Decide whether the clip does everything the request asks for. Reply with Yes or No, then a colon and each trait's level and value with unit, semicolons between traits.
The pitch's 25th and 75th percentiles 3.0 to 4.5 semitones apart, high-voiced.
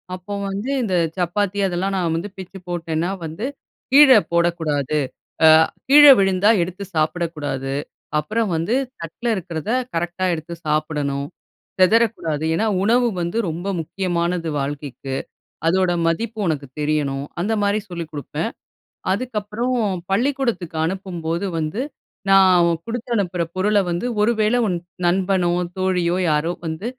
No: average, 4.0 semitones; medium, 175 Hz